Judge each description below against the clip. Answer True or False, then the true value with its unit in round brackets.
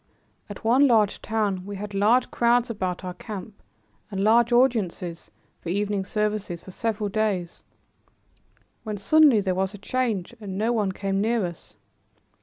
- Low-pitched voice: False (210 Hz)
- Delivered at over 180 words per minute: False (155 wpm)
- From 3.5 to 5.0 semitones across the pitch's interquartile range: False (3.0 semitones)